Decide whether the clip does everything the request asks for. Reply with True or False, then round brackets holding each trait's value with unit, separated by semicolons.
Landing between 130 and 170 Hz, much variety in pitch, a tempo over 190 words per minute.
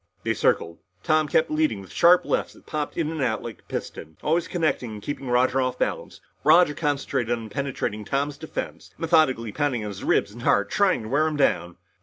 True (140 Hz; 5.8 semitones; 205 wpm)